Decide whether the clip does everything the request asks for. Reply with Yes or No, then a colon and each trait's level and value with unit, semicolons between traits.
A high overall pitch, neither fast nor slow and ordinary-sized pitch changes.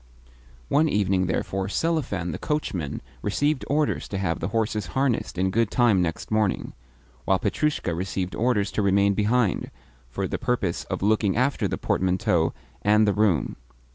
No: low, 100 Hz; average, 155 wpm; average, 4.4 semitones